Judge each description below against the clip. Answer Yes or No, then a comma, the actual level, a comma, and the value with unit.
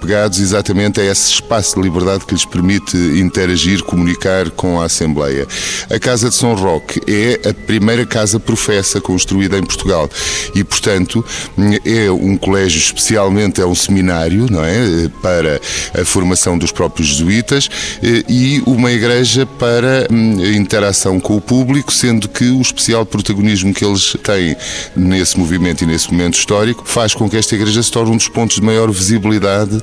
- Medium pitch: No, low, 100 Hz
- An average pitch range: Yes, average, 3.8 semitones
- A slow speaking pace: No, average, 160 wpm